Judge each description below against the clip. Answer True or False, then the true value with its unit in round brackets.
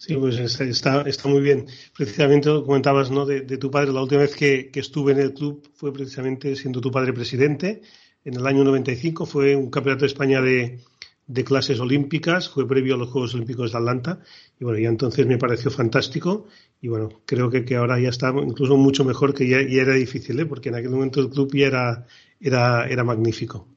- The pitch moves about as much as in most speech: False (1.8 semitones)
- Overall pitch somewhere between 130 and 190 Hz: True (135 Hz)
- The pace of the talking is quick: True (215 wpm)